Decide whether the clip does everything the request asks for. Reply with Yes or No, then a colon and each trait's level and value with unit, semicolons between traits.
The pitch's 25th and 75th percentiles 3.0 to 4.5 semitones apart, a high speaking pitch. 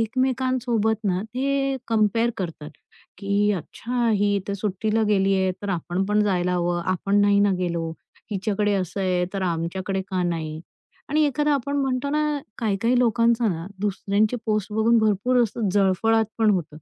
Yes: average, 3.7 semitones; high, 205 Hz